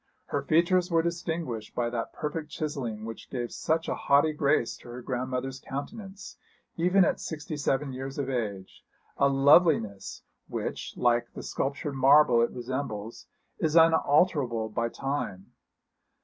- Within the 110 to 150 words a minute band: Yes, average, 140 wpm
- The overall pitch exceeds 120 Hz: Yes, low, 135 Hz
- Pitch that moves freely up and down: No, average, 4.9 semitones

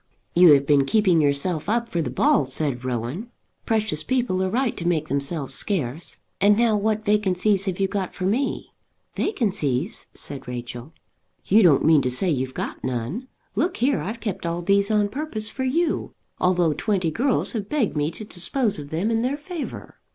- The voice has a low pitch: No, medium, 185 Hz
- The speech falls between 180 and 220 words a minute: Yes, average, 185 wpm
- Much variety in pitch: Yes, wide, 6.9 semitones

